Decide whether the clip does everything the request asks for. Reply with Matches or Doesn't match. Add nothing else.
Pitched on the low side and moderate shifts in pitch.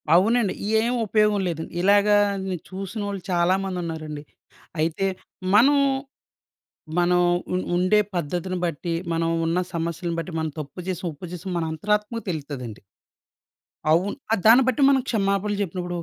Doesn't match